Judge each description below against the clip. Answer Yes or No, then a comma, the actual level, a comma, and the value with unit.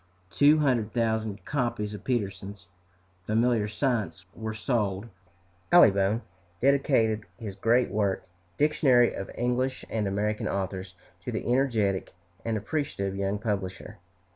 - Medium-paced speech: No, slow, 115 wpm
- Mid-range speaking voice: No, low, 110 Hz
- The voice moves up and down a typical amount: Yes, average, 3.7 semitones